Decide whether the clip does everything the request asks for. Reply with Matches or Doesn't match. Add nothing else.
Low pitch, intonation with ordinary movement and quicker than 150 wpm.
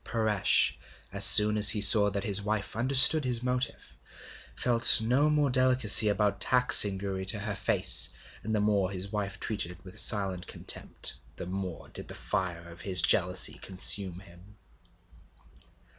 Matches